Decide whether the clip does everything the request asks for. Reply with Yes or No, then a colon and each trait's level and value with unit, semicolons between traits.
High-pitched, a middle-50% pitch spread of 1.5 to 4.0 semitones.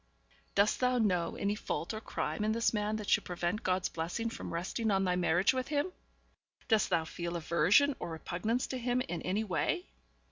No: high, 205 Hz; average, 4.8 semitones